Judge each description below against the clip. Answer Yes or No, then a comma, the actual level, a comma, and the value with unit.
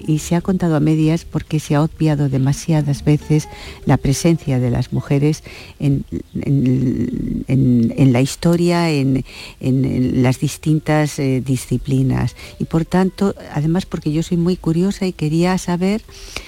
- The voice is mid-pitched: Yes, medium, 150 Hz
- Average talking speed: Yes, average, 155 wpm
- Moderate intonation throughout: Yes, average, 4.1 semitones